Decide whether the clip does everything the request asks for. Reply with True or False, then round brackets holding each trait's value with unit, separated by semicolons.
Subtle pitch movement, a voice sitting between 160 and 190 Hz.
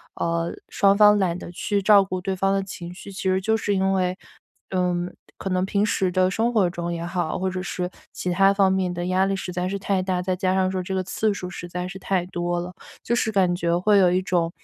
True (1.5 semitones; 185 Hz)